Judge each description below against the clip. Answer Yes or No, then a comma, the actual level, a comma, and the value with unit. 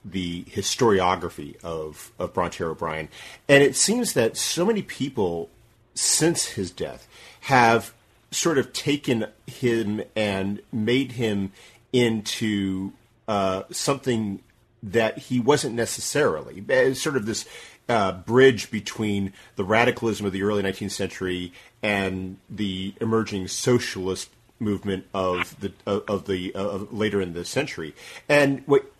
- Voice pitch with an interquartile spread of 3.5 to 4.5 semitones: Yes, average, 3.8 semitones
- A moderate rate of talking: No, slow, 130 wpm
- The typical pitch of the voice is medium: No, low, 105 Hz